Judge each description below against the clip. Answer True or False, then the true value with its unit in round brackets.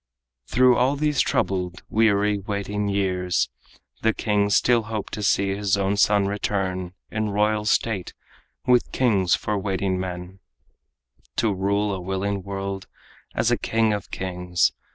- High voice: False (100 Hz)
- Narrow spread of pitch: True (2.0 semitones)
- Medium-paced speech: False (130 wpm)